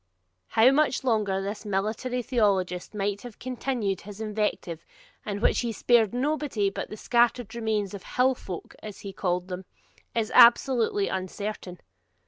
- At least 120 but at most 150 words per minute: Yes, average, 145 wpm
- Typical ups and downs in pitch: Yes, average, 3.5 semitones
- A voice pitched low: No, high, 215 Hz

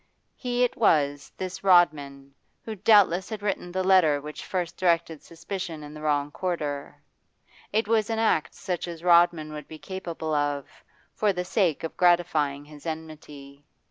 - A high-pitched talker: No, medium, 170 Hz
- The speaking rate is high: No, average, 160 wpm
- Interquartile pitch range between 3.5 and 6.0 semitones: Yes, average, 4.1 semitones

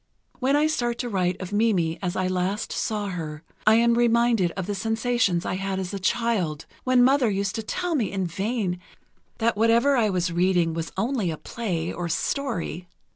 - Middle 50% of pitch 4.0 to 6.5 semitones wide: Yes, average, 4.8 semitones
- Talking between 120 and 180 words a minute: No, average, 195 wpm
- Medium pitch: No, high, 200 Hz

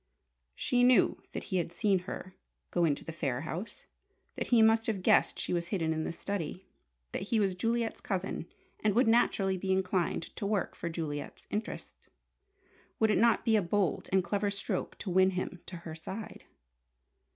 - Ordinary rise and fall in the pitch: Yes, average, 3.8 semitones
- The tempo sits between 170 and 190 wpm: Yes, average, 185 wpm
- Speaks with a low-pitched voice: No, high, 190 Hz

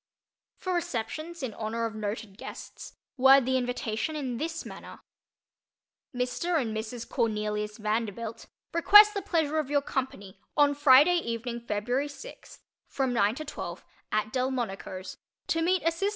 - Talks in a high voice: Yes, very high, 255 Hz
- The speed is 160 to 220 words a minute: No, average, 140 wpm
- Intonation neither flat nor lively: No, wide, 6.0 semitones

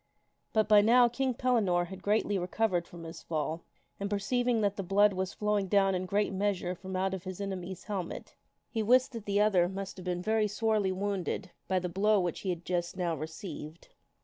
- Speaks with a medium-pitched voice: No, high, 195 Hz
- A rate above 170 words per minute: Yes, average, 200 wpm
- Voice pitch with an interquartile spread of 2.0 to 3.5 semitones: Yes, average, 2.7 semitones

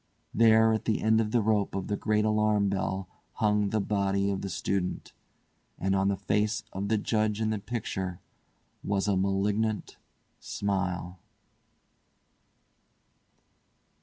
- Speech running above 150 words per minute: No, slow, 135 wpm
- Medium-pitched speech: No, low, 100 Hz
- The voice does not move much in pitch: Yes, narrow, 1.8 semitones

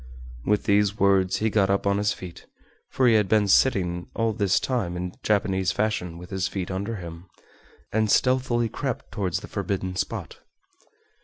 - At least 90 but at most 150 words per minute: No, average, 170 wpm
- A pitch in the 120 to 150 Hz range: No, low, 100 Hz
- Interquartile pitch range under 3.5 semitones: Yes, average, 2.7 semitones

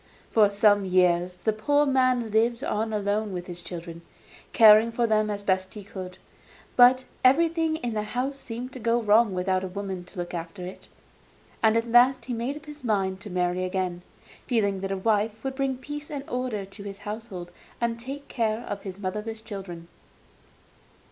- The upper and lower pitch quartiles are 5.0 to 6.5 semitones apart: No, average, 4.3 semitones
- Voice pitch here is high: Yes, high, 215 Hz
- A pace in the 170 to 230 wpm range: Yes, average, 185 wpm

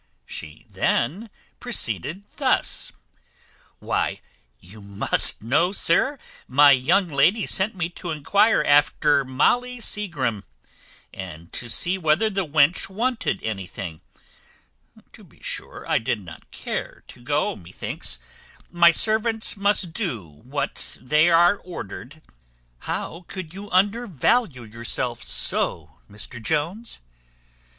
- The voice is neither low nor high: Yes, medium, 160 Hz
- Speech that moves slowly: Yes, slow, 115 wpm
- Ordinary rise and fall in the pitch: No, wide, 9.0 semitones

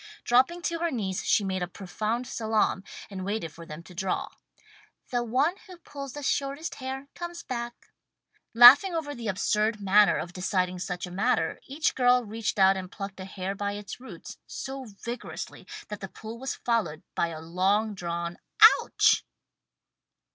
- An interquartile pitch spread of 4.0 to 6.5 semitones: Yes, wide, 5.4 semitones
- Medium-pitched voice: No, high, 215 Hz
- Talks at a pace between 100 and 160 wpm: No, average, 170 wpm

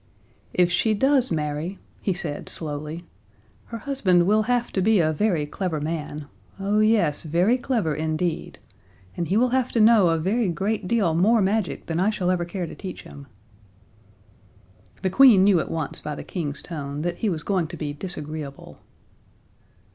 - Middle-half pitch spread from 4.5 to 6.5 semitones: Yes, average, 5.3 semitones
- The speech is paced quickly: No, average, 175 wpm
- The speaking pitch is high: No, medium, 180 Hz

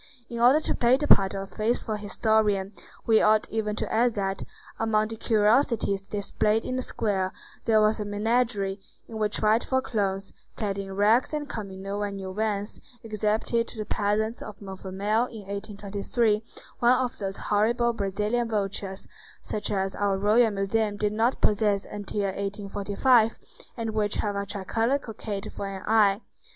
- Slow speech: No, average, 165 wpm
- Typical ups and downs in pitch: No, narrow, 2.0 semitones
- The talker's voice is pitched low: No, high, 210 Hz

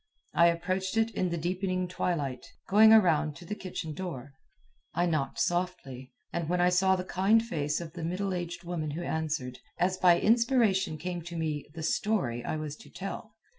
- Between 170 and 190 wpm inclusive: Yes, average, 185 wpm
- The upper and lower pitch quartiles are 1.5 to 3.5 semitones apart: Yes, average, 3.2 semitones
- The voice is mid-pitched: Yes, medium, 175 Hz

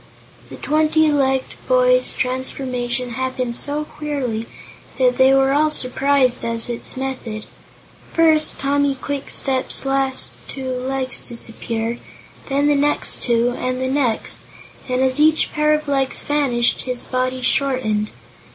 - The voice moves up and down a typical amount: No, narrow, 2.2 semitones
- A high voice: Yes, very high, 265 Hz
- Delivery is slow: Yes, slow, 130 wpm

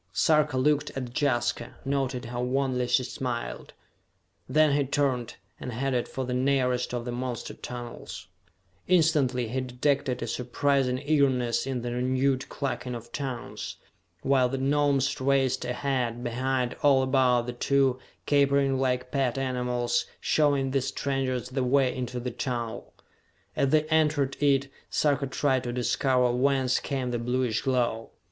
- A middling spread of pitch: No, narrow, 2.0 semitones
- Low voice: Yes, low, 130 Hz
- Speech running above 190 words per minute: No, average, 145 wpm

